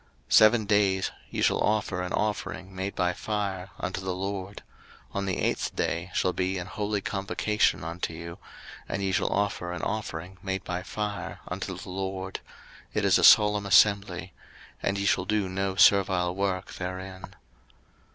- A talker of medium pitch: No, very low, 95 Hz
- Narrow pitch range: Yes, narrow, 1.6 semitones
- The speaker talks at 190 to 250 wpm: No, average, 165 wpm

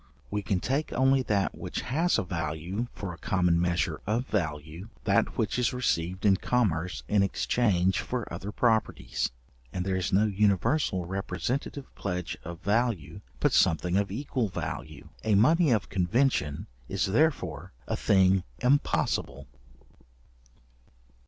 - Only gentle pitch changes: No, average, 5.1 semitones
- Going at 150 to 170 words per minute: No, average, 140 wpm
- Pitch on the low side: Yes, low, 100 Hz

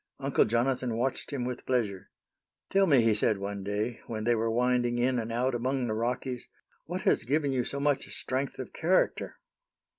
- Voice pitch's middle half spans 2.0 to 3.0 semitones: Yes, narrow, 2.6 semitones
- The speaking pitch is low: Yes, low, 125 Hz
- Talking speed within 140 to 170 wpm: No, average, 185 wpm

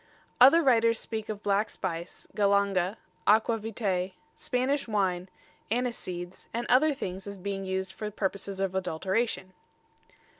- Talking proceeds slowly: Yes, slow, 125 wpm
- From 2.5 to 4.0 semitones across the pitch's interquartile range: Yes, average, 3.4 semitones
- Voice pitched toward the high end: Yes, high, 200 Hz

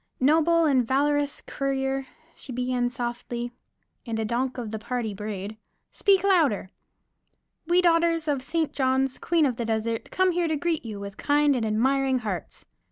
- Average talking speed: Yes, average, 160 wpm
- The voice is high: Yes, very high, 265 Hz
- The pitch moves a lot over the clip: No, average, 4.8 semitones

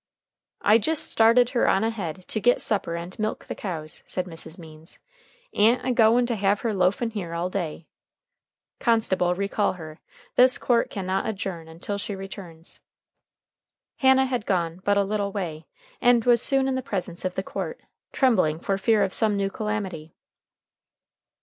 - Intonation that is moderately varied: Yes, average, 4.3 semitones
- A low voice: No, high, 200 Hz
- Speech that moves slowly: No, average, 170 wpm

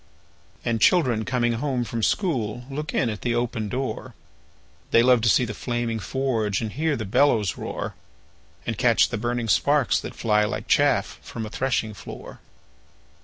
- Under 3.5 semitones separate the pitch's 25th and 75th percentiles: Yes, average, 2.9 semitones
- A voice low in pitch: Yes, low, 120 Hz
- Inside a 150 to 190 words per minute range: Yes, average, 170 wpm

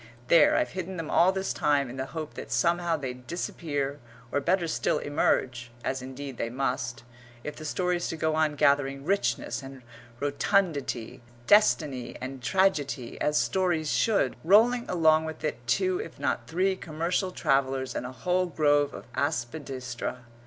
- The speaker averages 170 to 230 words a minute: No, average, 160 wpm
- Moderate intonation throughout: Yes, average, 4.8 semitones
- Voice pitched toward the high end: No, medium, 150 Hz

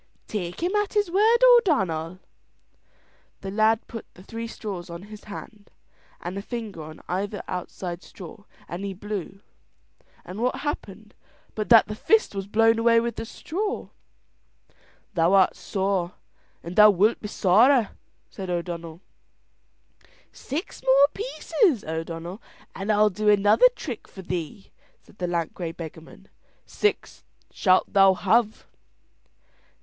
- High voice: Yes, high, 205 Hz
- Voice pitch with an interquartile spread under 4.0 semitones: No, average, 4.3 semitones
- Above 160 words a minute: No, slow, 135 wpm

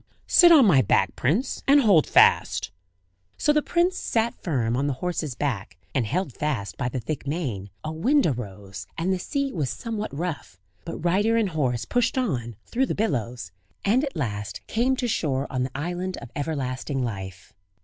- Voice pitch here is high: No, medium, 150 Hz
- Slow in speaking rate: No, average, 180 wpm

